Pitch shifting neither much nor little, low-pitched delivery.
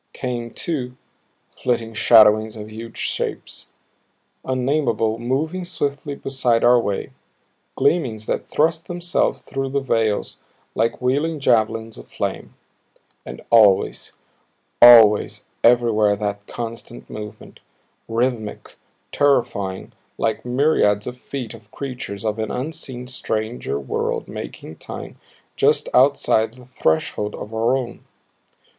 Yes: average, 3.4 semitones; low, 120 Hz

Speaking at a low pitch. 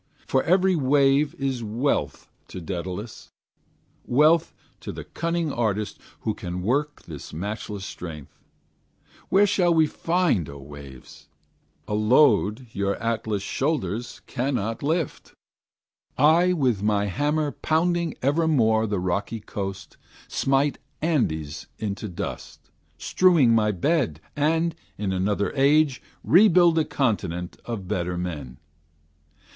Yes: low, 115 Hz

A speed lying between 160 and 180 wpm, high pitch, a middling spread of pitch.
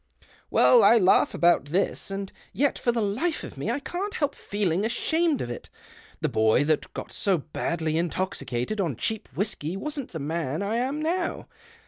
No: average, 175 wpm; high, 200 Hz; wide, 8.9 semitones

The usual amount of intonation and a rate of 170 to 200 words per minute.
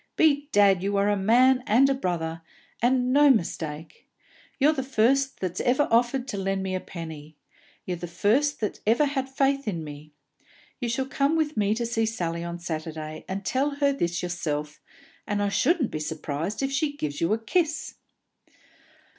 No: wide, 7.8 semitones; average, 180 wpm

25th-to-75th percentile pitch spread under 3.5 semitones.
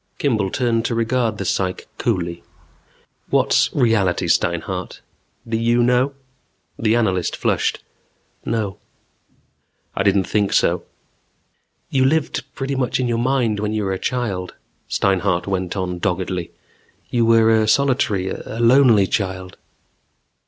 No: average, 4.2 semitones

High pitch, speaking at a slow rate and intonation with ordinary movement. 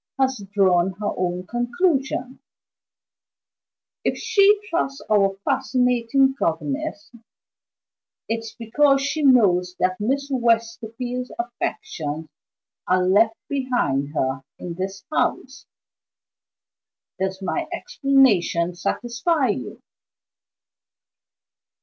No: high, 235 Hz; slow, 85 wpm; wide, 6.3 semitones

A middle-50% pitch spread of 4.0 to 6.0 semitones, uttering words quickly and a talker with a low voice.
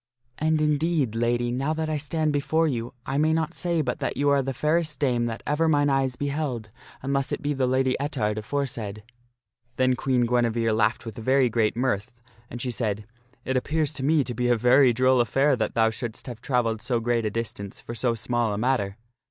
No: average, 3.6 semitones; fast, 215 wpm; low, 125 Hz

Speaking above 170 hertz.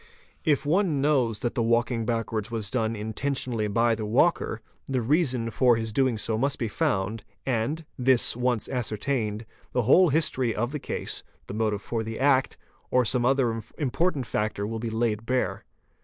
No: low, 120 Hz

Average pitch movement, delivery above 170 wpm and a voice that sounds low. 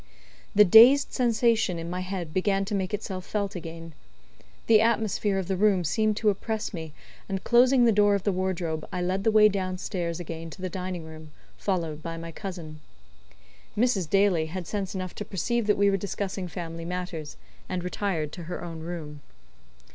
No: average, 3.6 semitones; average, 185 wpm; medium, 185 Hz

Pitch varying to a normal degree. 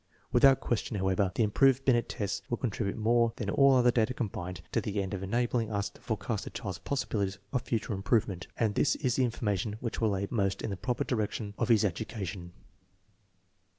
Yes: average, 3.3 semitones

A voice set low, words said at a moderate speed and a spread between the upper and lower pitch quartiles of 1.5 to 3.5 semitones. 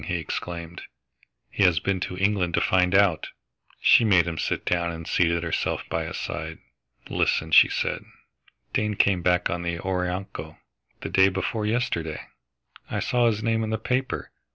Yes: very low, 90 Hz; average, 170 wpm; average, 3.2 semitones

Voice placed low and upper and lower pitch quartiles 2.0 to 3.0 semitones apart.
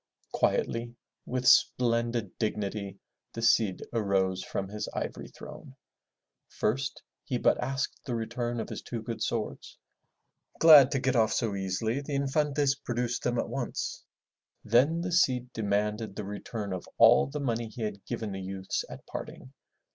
No: low, 115 Hz; average, 3.5 semitones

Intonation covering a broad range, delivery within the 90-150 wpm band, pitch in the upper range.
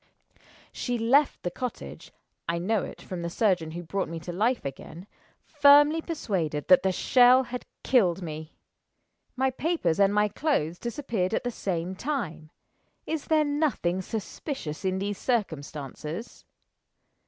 Yes: wide, 7.2 semitones; average, 140 wpm; high, 200 Hz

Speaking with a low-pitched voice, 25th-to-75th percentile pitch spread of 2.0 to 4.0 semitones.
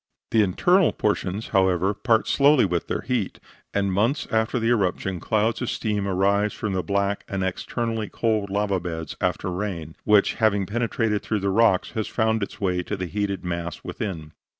Yes: low, 100 Hz; average, 2.9 semitones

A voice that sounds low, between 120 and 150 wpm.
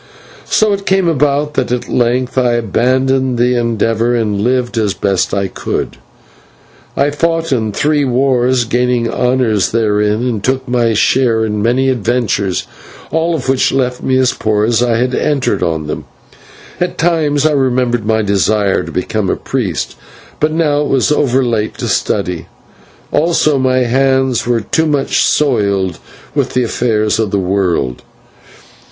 No: low, 125 Hz; average, 160 wpm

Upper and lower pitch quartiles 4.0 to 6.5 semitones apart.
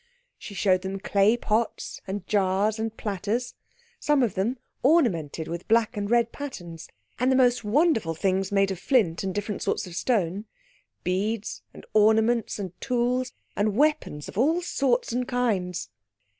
Yes: average, 4.4 semitones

